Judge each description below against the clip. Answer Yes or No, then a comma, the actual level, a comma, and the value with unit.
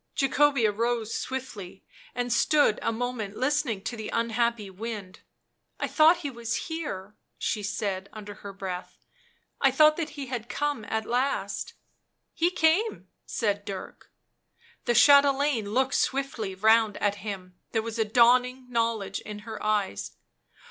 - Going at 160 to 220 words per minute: No, average, 150 wpm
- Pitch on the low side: No, high, 230 Hz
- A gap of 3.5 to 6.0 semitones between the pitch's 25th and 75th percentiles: Yes, average, 4.3 semitones